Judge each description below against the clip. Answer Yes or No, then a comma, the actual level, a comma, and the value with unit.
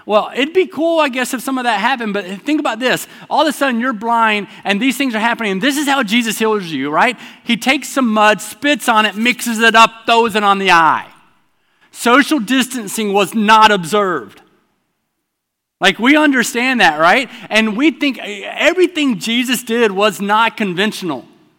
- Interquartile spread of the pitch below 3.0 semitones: No, average, 3.9 semitones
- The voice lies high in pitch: Yes, high, 230 Hz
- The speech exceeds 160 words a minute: Yes, average, 190 wpm